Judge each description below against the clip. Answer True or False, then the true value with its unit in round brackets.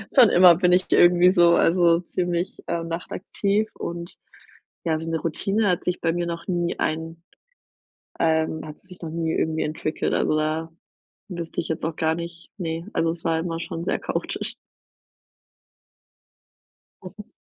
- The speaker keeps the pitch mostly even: True (1.6 semitones)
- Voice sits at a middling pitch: True (170 Hz)